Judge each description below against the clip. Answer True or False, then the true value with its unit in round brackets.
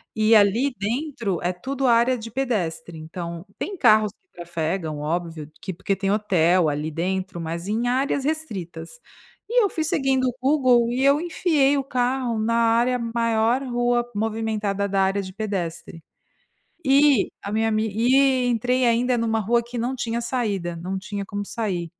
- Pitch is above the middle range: True (225 Hz)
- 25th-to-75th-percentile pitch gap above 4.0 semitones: True (4.9 semitones)